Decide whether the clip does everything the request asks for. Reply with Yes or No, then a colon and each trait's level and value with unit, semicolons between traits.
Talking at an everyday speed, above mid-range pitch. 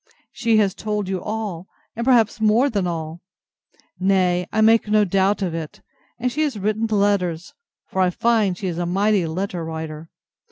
Yes: average, 175 wpm; high, 195 Hz